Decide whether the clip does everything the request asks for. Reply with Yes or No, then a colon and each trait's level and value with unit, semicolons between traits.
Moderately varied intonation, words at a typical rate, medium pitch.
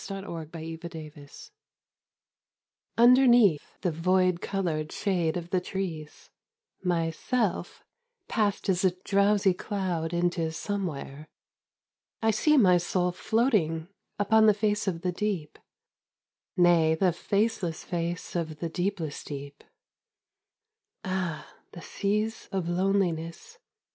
No: average, 3.8 semitones; slow, 120 wpm; medium, 180 Hz